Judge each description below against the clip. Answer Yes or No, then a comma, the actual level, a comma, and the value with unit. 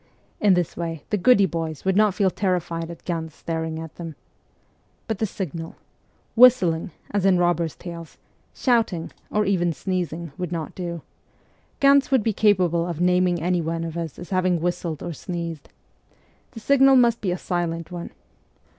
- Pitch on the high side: No, medium, 175 Hz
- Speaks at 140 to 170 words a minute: Yes, average, 165 wpm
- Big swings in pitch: No, average, 2.8 semitones